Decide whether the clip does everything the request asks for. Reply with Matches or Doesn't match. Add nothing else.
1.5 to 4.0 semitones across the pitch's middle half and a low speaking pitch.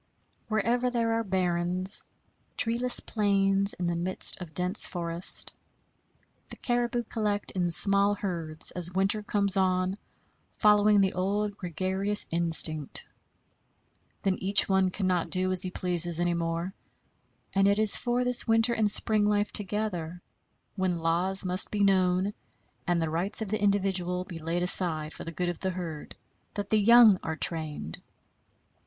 Doesn't match